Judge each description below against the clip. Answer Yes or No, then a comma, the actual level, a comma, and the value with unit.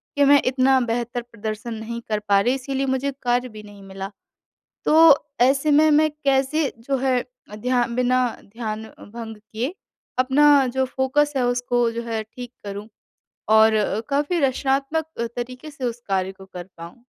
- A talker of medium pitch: No, high, 245 Hz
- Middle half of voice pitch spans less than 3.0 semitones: No, average, 3.6 semitones